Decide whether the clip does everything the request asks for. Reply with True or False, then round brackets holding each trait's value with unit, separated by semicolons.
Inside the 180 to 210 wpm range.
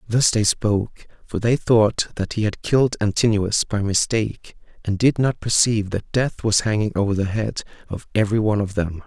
True (190 wpm)